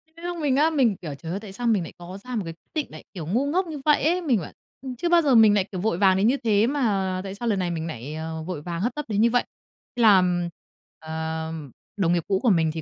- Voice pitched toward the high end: Yes, high, 200 Hz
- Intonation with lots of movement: Yes, wide, 6.6 semitones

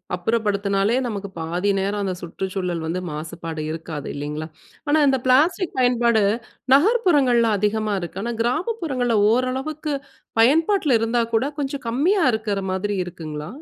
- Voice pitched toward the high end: Yes, high, 225 Hz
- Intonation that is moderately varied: No, wide, 6.4 semitones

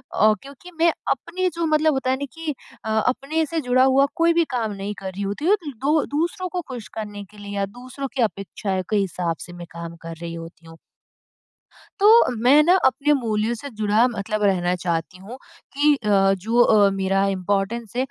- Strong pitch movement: Yes, wide, 6.4 semitones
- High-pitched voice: Yes, high, 225 Hz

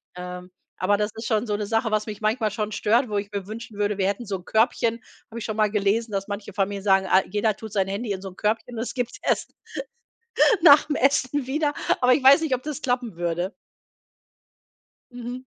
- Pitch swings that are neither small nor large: Yes, average, 3.4 semitones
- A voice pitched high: Yes, high, 215 Hz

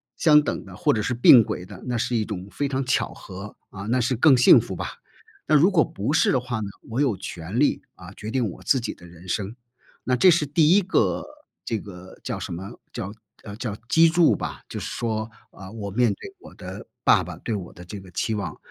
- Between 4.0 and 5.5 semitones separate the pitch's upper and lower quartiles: Yes, average, 5.2 semitones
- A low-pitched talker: Yes, low, 115 Hz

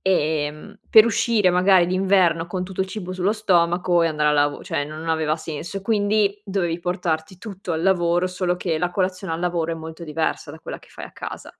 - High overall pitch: No, medium, 175 Hz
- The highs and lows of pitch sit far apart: No, average, 2.8 semitones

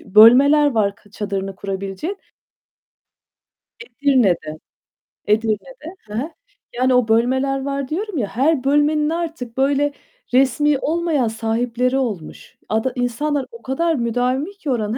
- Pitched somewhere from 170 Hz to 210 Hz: No, very high, 255 Hz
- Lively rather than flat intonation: No, average, 4.8 semitones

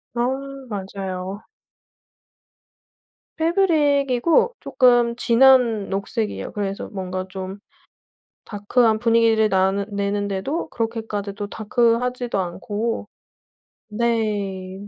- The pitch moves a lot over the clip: No, average, 3.3 semitones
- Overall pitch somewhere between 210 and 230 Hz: Yes, high, 215 Hz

